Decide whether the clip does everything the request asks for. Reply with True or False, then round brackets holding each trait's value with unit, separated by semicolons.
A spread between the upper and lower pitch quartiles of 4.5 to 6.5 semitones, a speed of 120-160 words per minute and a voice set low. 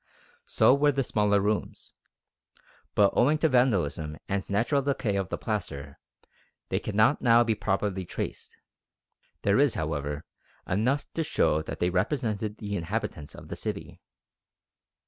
True (5.2 semitones; 140 wpm; 105 Hz)